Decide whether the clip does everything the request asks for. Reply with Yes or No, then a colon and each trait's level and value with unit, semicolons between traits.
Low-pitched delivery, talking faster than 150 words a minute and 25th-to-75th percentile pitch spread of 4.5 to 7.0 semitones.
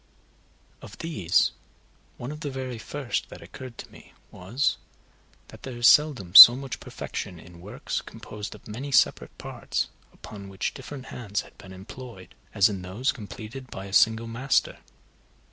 Yes: low, 115 Hz; average, 160 wpm; average, 4.9 semitones